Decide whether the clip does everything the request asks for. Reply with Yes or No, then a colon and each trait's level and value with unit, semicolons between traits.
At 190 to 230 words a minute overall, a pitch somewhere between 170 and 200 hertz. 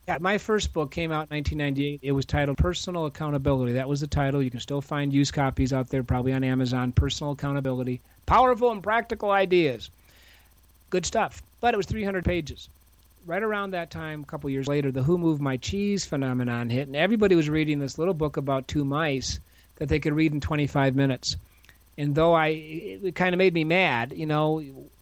No: average, 200 wpm; medium, 145 Hz